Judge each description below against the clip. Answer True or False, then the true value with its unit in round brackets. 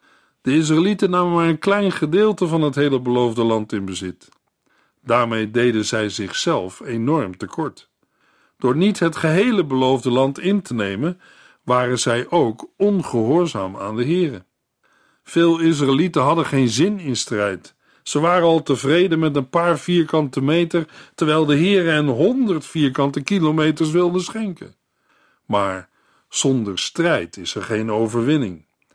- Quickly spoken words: False (140 wpm)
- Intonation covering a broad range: True (5.9 semitones)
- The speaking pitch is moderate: True (150 Hz)